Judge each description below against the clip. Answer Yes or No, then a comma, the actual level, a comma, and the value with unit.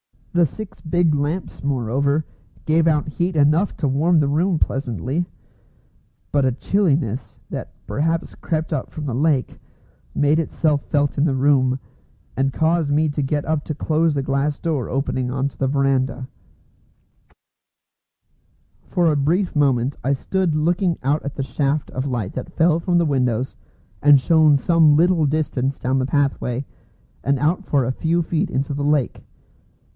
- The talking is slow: No, average, 160 wpm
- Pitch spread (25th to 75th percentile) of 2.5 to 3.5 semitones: Yes, average, 3.0 semitones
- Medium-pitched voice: Yes, medium, 145 Hz